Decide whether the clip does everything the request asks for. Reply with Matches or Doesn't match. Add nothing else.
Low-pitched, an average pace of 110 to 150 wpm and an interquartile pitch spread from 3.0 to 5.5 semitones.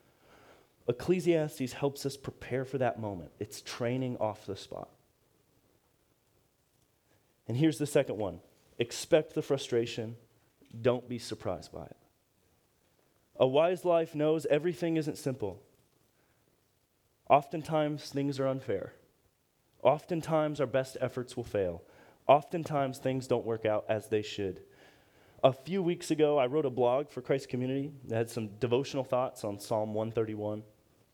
Matches